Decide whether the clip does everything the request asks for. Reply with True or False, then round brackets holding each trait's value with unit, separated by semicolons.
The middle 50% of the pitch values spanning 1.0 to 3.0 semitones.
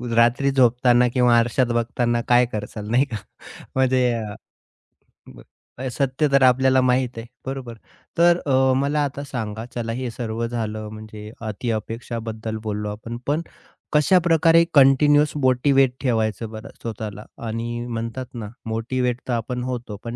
True (2.7 semitones)